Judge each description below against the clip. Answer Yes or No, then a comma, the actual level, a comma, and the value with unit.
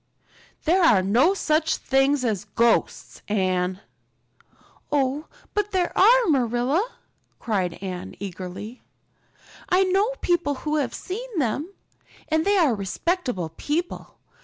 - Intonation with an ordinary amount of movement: No, wide, 9.0 semitones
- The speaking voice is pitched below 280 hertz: No, very high, 285 Hz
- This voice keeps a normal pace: No, slow, 115 wpm